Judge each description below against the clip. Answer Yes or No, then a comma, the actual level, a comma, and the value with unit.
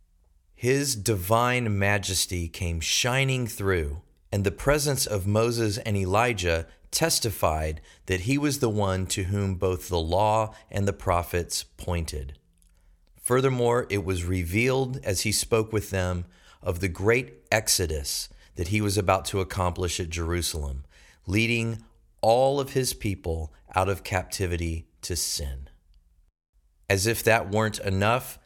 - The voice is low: Yes, very low, 95 Hz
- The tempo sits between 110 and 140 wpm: Yes, slow, 135 wpm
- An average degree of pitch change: Yes, average, 4.9 semitones